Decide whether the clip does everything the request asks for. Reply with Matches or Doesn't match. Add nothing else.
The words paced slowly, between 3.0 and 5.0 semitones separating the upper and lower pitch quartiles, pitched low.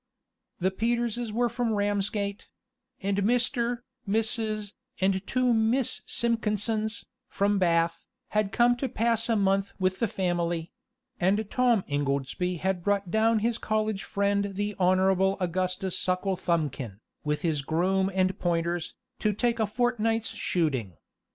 Doesn't match